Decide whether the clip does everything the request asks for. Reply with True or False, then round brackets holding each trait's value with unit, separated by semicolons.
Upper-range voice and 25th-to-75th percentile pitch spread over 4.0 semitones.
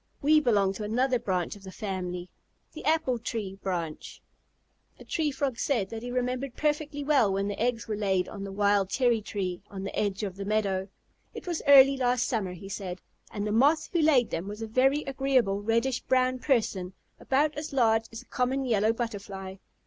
True (225 Hz; 5.1 semitones)